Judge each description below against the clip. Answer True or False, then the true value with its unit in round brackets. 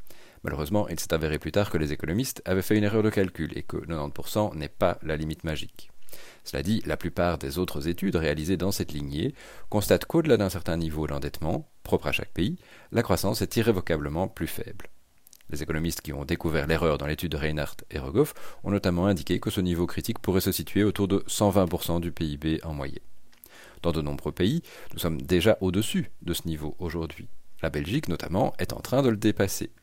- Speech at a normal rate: True (200 wpm)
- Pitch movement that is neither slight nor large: True (4.1 semitones)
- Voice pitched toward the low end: True (85 Hz)